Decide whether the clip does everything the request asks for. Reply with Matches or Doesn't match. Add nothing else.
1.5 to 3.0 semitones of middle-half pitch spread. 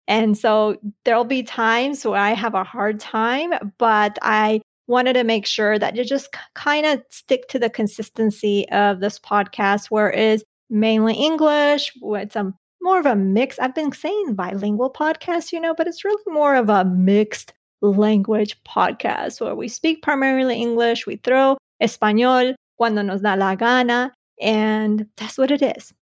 Doesn't match